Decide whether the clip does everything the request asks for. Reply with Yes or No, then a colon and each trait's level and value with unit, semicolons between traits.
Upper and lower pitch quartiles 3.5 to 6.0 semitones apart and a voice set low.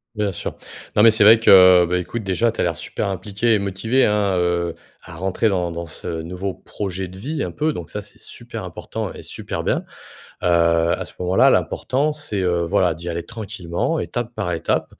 Yes: average, 3.9 semitones; very low, 95 Hz